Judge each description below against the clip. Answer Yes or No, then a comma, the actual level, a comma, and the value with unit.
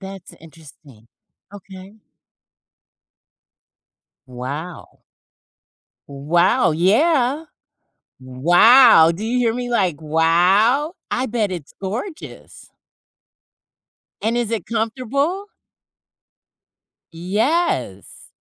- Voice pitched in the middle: No, high, 200 Hz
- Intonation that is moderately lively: No, wide, 7.0 semitones